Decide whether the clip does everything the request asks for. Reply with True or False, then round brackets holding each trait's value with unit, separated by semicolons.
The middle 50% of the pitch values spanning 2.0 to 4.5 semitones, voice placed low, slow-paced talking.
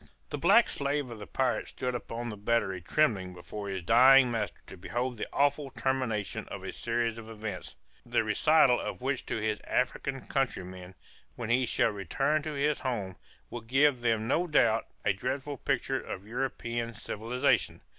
False (4.0 semitones; 120 Hz; 170 wpm)